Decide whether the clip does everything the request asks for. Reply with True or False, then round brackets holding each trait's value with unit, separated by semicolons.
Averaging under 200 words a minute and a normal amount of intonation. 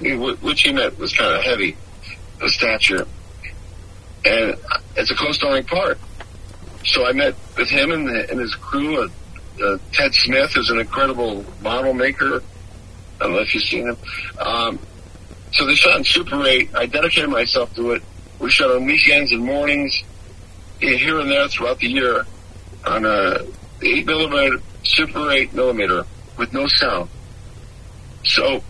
False (155 wpm; 6.5 semitones)